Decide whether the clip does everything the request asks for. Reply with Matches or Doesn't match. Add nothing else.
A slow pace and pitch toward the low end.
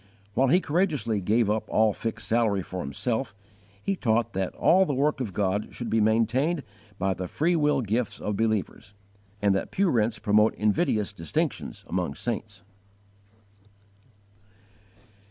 Doesn't match